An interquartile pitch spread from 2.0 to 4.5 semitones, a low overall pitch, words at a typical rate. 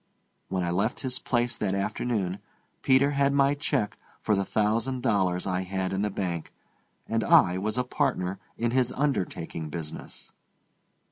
No: average, 5.2 semitones; low, 105 Hz; average, 155 wpm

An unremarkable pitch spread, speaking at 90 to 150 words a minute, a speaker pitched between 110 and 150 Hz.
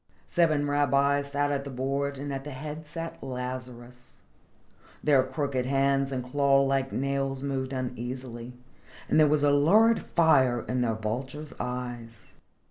No: narrow, 2.2 semitones; average, 145 wpm; low, 135 Hz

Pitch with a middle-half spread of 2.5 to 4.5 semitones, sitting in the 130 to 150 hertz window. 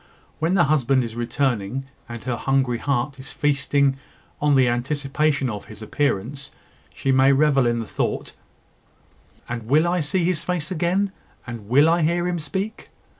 Yes: average, 4.2 semitones; medium, 140 Hz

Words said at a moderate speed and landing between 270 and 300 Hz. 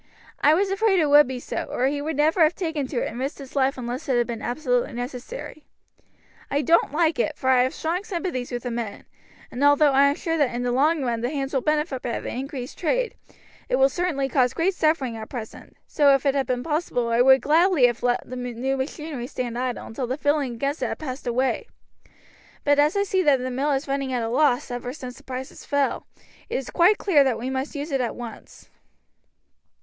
No: fast, 230 wpm; very high, 275 Hz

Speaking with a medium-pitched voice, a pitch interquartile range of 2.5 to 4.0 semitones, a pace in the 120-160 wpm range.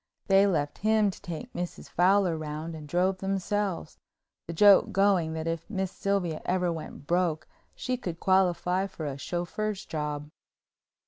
Yes: medium, 180 Hz; average, 3.4 semitones; average, 150 wpm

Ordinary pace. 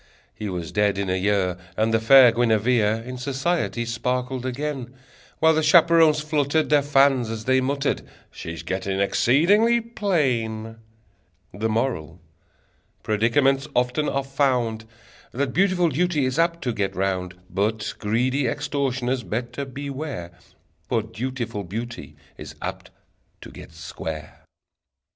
No: slow, 130 wpm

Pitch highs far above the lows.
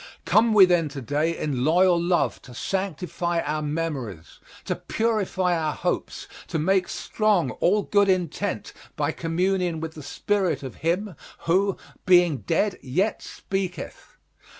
No: average, 3.9 semitones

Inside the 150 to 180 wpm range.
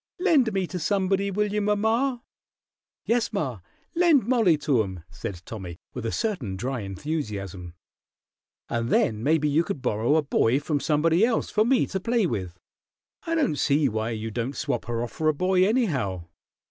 Yes: average, 175 wpm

